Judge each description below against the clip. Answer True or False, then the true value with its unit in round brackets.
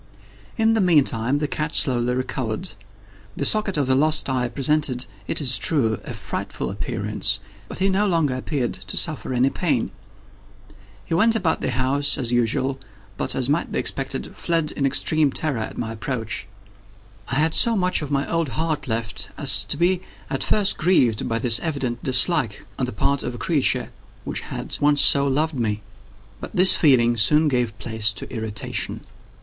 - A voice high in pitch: False (135 Hz)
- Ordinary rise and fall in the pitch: True (4.9 semitones)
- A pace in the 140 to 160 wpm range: False (175 wpm)